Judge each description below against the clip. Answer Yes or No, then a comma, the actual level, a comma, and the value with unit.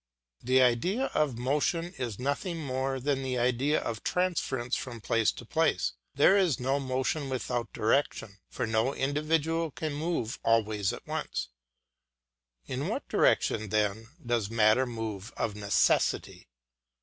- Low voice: Yes, low, 130 Hz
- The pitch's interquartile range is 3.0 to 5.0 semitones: Yes, average, 4.5 semitones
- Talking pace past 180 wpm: No, average, 140 wpm